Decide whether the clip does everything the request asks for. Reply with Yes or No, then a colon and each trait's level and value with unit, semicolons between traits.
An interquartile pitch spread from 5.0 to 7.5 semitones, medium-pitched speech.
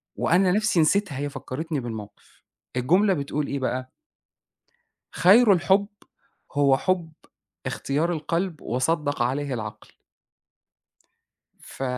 Yes: average, 5.3 semitones; medium, 150 Hz